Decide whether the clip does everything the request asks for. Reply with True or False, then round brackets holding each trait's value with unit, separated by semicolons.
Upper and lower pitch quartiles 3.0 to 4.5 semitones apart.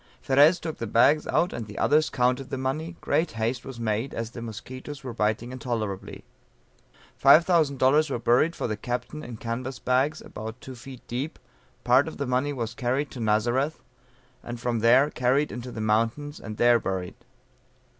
True (3.4 semitones)